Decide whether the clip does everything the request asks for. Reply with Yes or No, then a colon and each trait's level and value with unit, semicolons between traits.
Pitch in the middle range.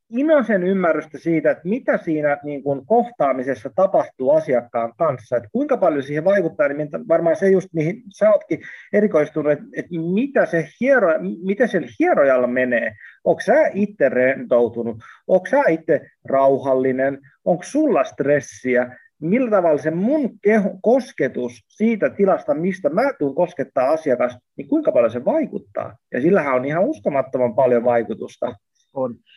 Yes: medium, 165 Hz